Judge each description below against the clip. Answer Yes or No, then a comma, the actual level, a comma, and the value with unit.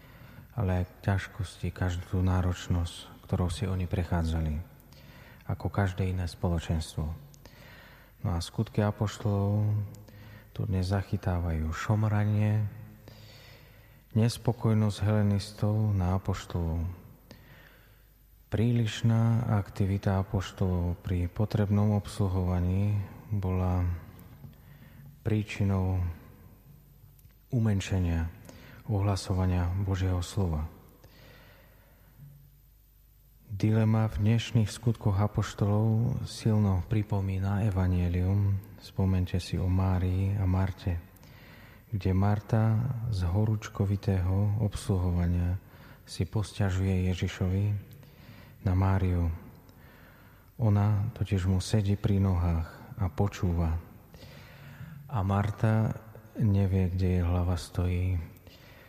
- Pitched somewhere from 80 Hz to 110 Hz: Yes, low, 100 Hz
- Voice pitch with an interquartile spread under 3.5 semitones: Yes, average, 3.1 semitones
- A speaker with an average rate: No, slow, 75 wpm